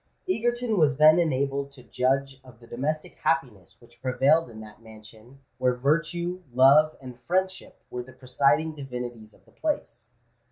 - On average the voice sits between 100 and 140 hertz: Yes, low, 135 Hz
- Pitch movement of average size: Yes, average, 4.1 semitones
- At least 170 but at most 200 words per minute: No, average, 155 wpm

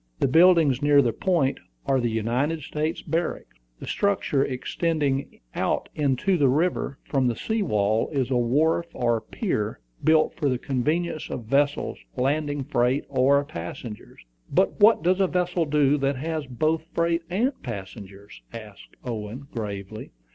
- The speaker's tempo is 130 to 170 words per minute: Yes, average, 150 wpm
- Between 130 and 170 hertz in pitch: Yes, medium, 140 Hz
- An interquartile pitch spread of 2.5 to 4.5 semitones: No, average, 5.1 semitones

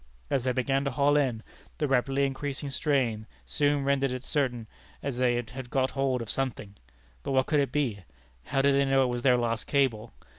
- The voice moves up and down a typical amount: No, narrow, 2.3 semitones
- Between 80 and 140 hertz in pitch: Yes, low, 135 Hz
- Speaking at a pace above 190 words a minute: Yes, average, 200 wpm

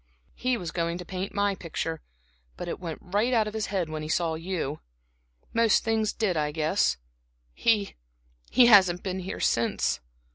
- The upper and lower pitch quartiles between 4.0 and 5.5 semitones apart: Yes, average, 4.5 semitones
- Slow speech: No, average, 170 wpm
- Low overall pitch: No, medium, 185 Hz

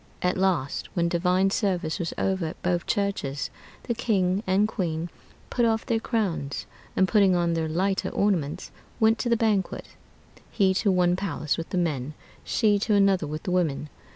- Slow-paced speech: No, average, 175 wpm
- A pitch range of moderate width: Yes, average, 3.3 semitones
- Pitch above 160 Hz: Yes, medium, 185 Hz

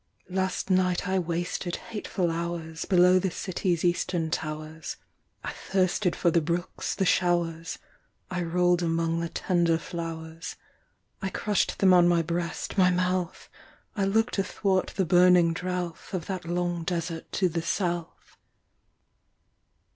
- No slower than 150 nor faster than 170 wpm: No, slow, 135 wpm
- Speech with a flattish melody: Yes, narrow, 1.7 semitones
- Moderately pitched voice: Yes, medium, 175 Hz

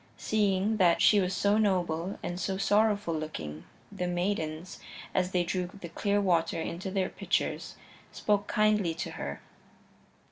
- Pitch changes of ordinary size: Yes, average, 3.2 semitones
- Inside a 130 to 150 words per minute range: Yes, average, 145 wpm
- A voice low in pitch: No, medium, 185 Hz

